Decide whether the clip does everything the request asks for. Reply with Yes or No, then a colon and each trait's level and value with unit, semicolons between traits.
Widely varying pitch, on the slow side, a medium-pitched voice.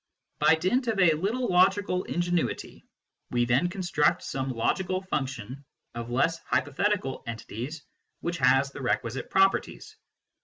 Yes: wide, 6.0 semitones; slow, 130 wpm; medium, 165 Hz